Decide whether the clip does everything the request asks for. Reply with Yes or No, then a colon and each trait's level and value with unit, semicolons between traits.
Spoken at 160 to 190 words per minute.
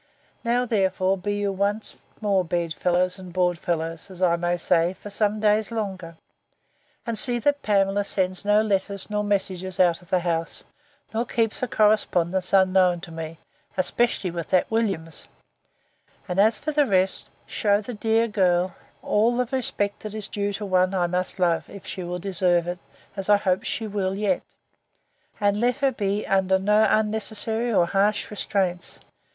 Yes: average, 170 wpm